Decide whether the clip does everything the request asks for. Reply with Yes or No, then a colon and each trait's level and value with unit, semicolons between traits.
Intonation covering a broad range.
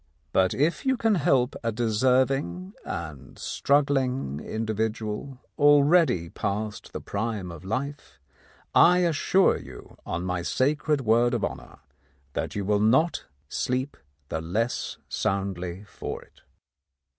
Yes: wide, 6.3 semitones